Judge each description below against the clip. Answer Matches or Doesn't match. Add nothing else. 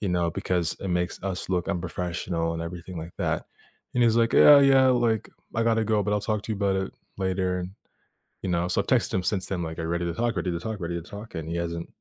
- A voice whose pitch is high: Doesn't match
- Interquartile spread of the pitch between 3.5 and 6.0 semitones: Matches